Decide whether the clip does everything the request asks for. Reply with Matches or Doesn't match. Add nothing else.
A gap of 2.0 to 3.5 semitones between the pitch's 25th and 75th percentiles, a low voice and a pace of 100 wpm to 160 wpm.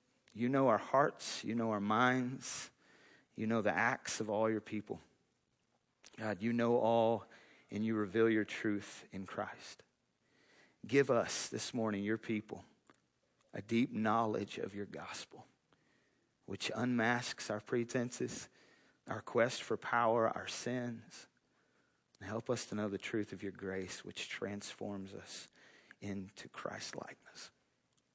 Matches